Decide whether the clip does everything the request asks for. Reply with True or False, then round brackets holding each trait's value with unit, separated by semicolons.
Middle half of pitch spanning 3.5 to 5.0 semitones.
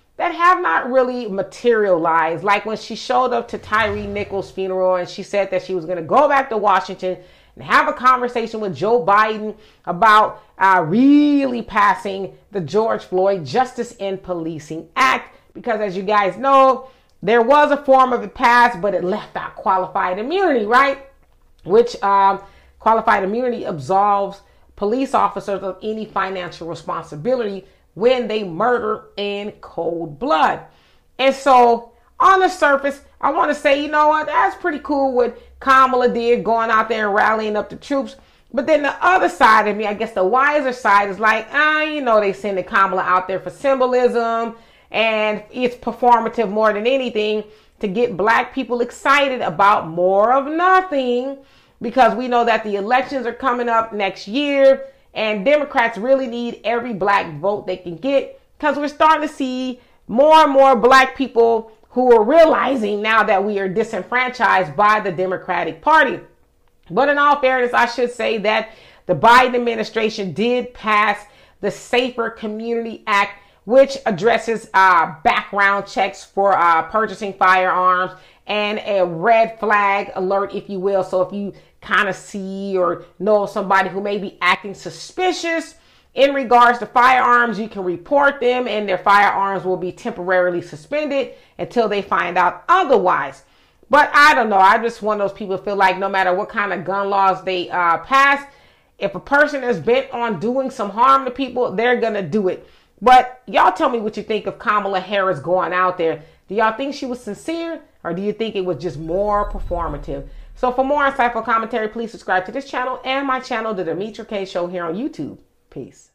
True (4.6 semitones)